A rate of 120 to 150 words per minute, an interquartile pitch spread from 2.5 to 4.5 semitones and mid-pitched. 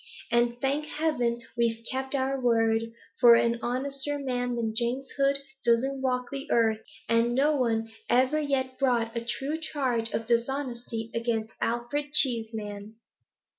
No: average, 140 wpm; average, 2.8 semitones; high, 240 Hz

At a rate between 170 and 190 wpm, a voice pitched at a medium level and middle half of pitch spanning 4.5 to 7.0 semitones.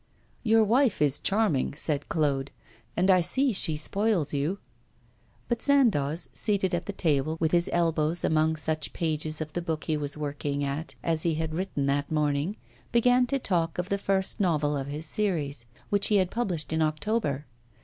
Yes: average, 180 wpm; medium, 160 Hz; average, 4.8 semitones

